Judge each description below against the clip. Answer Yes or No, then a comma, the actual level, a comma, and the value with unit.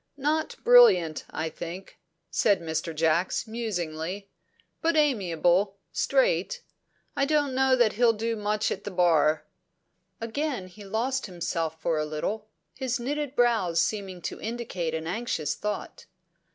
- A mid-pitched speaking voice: No, high, 205 Hz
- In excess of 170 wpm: No, slow, 135 wpm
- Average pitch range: No, wide, 6.7 semitones